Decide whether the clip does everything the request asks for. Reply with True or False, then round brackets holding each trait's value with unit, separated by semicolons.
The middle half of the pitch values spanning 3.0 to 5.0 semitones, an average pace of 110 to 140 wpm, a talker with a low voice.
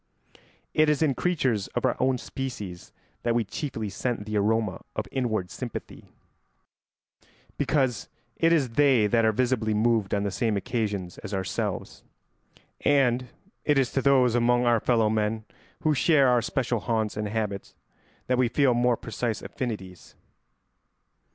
False (3.3 semitones; 150 wpm; 120 Hz)